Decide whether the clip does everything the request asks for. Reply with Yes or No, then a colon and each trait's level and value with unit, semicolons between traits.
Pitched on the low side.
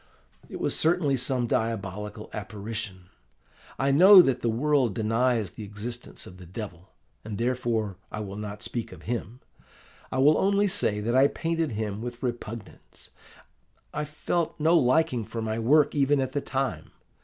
Yes: low, 120 Hz